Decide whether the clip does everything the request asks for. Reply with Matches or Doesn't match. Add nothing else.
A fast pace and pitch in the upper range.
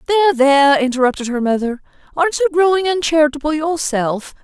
Doesn't match